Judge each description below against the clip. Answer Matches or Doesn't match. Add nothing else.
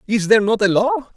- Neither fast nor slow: Doesn't match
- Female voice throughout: Doesn't match